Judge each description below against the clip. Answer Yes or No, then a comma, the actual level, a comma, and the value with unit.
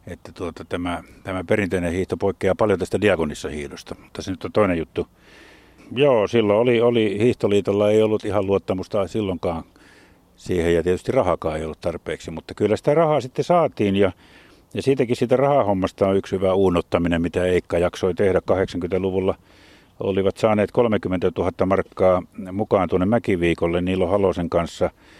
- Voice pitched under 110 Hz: Yes, very low, 95 Hz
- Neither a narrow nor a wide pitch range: Yes, average, 3.3 semitones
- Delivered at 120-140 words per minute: No, fast, 155 wpm